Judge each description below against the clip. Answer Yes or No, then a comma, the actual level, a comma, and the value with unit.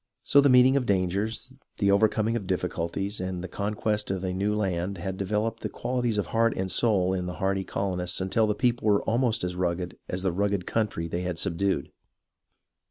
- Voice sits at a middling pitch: No, low, 100 Hz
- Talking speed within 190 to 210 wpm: Yes, average, 195 wpm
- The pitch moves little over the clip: No, average, 3.1 semitones